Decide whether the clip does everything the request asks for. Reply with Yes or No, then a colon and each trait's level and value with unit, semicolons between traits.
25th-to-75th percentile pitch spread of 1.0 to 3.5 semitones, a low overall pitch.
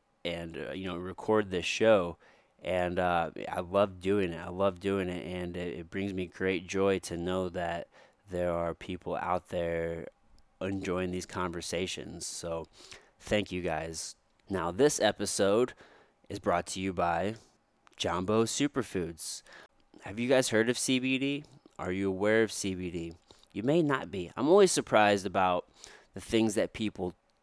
Yes: average, 2.9 semitones; very low, 95 Hz